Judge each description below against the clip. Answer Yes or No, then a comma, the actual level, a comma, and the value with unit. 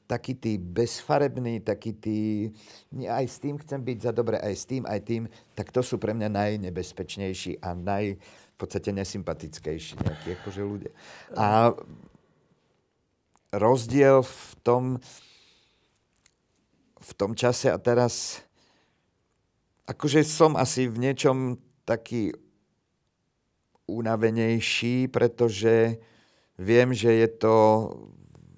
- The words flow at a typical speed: No, slow, 105 wpm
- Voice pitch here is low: Yes, low, 115 Hz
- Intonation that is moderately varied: Yes, average, 3.3 semitones